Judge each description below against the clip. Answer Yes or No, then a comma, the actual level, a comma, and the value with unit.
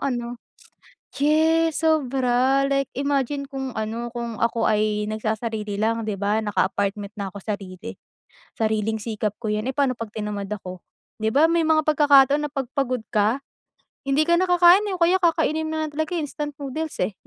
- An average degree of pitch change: No, wide, 5.7 semitones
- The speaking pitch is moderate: No, very high, 255 Hz